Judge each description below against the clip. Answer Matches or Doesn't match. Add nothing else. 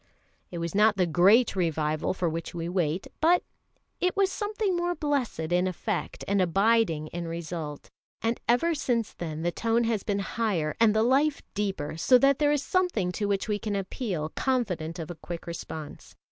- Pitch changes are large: Matches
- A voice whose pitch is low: Doesn't match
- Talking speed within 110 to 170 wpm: Doesn't match